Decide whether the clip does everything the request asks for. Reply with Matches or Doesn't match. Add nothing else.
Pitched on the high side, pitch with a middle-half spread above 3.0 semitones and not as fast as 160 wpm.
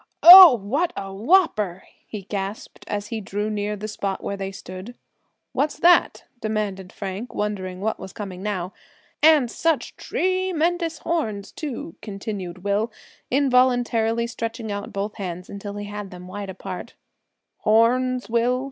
Matches